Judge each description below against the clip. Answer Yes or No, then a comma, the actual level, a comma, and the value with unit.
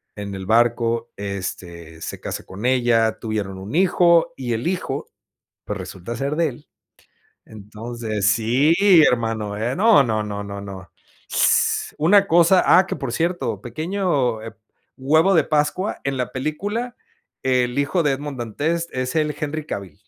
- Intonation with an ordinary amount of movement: No, wide, 6.4 semitones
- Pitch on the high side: No, low, 125 Hz